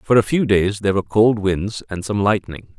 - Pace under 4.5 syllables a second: No, 5.3 syllables/s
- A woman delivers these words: No, male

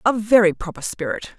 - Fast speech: No, average, 175 wpm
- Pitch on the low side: No, high, 195 Hz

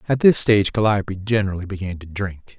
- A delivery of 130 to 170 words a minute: No, average, 185 wpm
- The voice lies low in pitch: Yes, low, 100 Hz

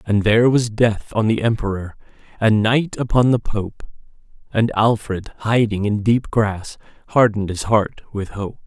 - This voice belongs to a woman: No, male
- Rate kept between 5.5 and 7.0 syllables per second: No, 4.5 syllables/s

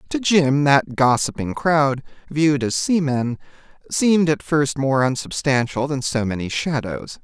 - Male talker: Yes, male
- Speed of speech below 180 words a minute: Yes, average, 140 wpm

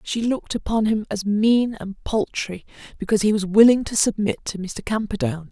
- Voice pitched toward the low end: No, high, 205 Hz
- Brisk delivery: No, average, 185 wpm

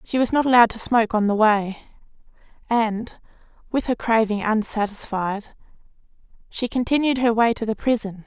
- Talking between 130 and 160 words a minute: Yes, average, 150 wpm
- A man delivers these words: No, female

